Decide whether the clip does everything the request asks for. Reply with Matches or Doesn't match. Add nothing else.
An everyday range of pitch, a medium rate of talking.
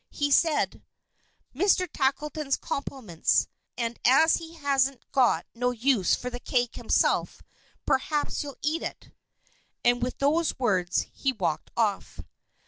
Doesn't match